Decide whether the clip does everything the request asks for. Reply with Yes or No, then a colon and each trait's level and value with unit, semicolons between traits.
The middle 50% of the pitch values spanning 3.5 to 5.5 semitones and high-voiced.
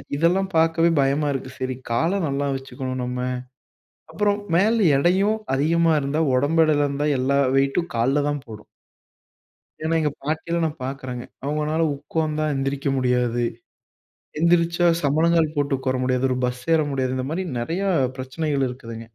No: average, 4.0 semitones; medium, 145 Hz